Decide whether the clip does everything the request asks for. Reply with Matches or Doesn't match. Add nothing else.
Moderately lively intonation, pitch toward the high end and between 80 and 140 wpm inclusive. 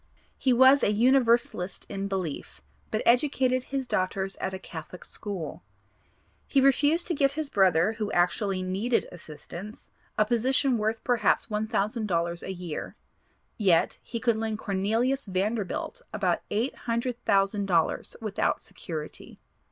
Matches